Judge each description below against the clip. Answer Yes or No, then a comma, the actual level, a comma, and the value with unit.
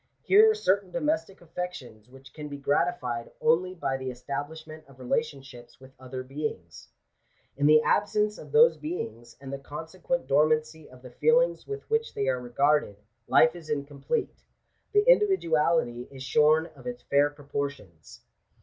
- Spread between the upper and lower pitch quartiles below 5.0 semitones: No, average, 5.3 semitones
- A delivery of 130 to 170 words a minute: Yes, average, 160 wpm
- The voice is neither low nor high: Yes, medium, 150 Hz